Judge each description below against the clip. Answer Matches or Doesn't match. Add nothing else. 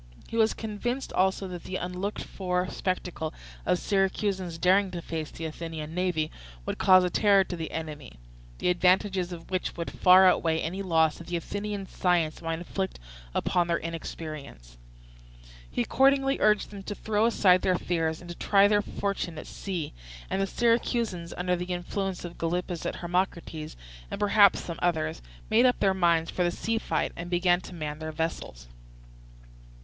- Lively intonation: Doesn't match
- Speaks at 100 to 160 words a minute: Doesn't match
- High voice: Doesn't match